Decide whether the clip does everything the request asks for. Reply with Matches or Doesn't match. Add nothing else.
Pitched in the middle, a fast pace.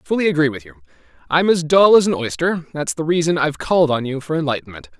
Matches